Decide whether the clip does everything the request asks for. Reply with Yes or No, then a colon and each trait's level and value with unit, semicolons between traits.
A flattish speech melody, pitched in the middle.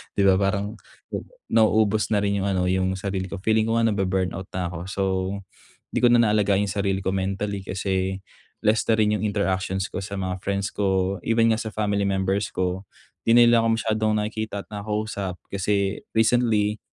No: narrow, 2.1 semitones; low, 100 Hz